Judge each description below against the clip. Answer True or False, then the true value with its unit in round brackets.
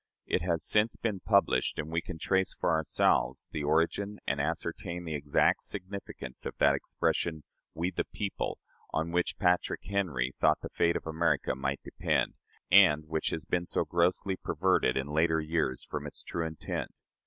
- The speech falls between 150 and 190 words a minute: True (170 wpm)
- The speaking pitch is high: False (85 Hz)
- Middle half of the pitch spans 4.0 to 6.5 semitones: False (3.0 semitones)